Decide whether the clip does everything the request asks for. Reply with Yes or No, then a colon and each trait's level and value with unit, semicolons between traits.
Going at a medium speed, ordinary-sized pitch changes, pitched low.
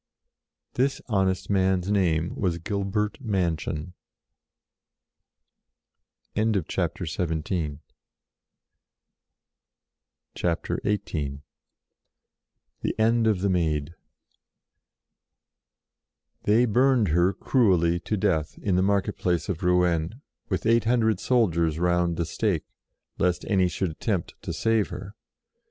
No: slow, 95 wpm; average, 3.9 semitones; very low, 95 Hz